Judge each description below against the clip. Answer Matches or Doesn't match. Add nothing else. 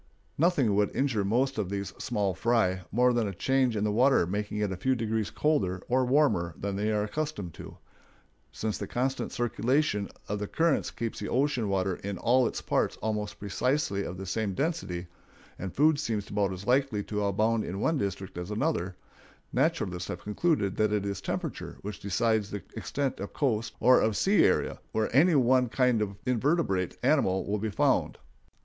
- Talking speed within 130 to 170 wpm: Doesn't match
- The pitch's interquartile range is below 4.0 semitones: Doesn't match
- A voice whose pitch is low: Matches